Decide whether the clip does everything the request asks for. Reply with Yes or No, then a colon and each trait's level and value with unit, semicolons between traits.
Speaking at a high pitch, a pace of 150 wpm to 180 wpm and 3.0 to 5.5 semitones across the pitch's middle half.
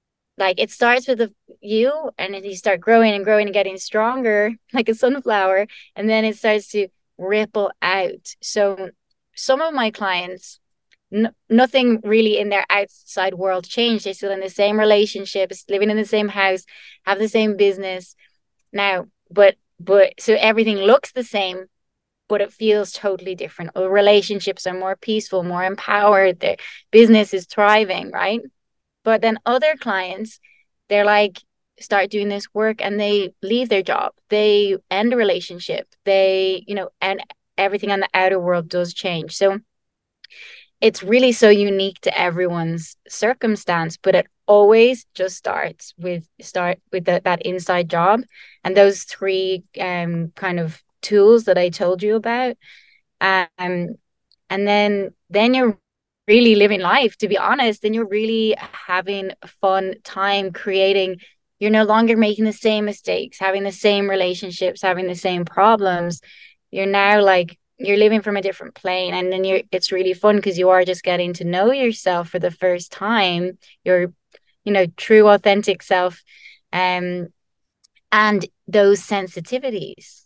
No: high, 200 Hz; average, 160 wpm; narrow, 2.5 semitones